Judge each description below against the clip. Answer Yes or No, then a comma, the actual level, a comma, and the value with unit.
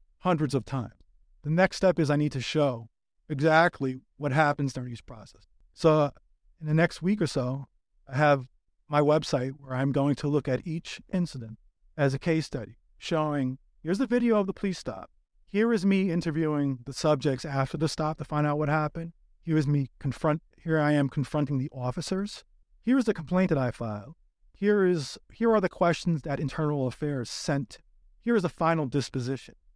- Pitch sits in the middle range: Yes, medium, 150 Hz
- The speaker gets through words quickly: No, average, 190 wpm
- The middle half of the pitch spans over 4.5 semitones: No, average, 3.9 semitones